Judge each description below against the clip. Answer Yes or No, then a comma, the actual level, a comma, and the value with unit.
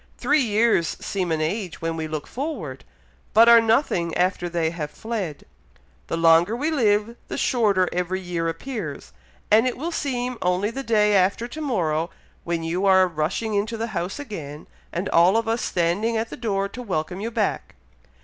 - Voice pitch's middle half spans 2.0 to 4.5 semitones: No, average, 5.3 semitones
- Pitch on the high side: Yes, high, 195 Hz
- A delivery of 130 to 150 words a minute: No, average, 180 wpm